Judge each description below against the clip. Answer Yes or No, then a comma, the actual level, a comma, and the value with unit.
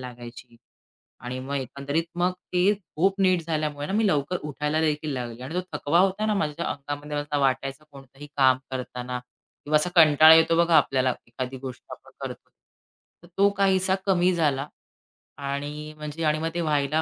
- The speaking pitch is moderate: Yes, medium, 150 Hz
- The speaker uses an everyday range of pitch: Yes, average, 3.7 semitones